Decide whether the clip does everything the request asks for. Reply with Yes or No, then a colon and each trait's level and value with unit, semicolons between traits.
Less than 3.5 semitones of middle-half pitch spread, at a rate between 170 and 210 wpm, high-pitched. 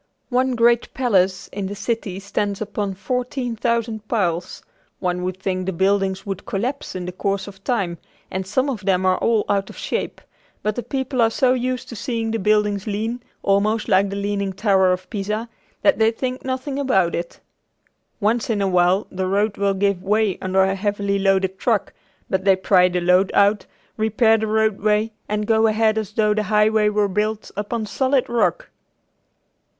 Yes: average, 2.8 semitones; average, 180 wpm; high, 210 Hz